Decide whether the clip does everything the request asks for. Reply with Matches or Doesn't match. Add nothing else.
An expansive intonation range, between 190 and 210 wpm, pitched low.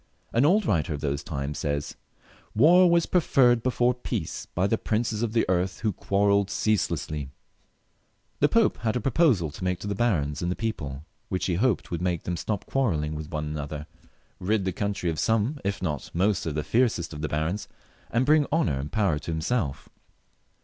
Matches